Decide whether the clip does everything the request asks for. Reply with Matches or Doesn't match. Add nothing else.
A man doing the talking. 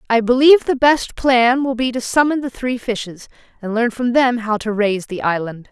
Doesn't match